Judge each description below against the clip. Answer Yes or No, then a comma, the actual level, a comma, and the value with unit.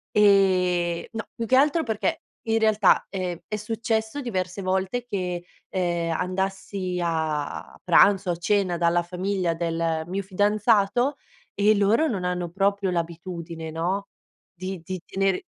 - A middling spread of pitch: Yes, average, 3.1 semitones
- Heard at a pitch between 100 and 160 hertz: No, high, 190 Hz